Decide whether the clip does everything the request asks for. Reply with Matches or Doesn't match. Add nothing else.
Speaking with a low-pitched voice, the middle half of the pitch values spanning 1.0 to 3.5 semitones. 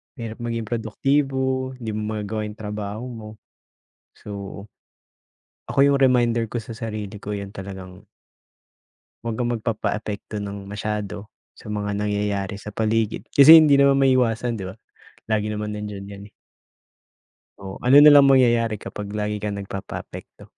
Matches